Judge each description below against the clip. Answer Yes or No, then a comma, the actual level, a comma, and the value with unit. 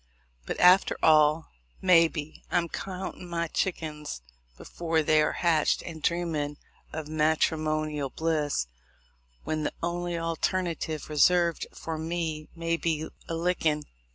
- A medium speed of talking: No, slow, 120 wpm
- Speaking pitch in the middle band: Yes, medium, 160 Hz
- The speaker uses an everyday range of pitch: No, narrow, 1.8 semitones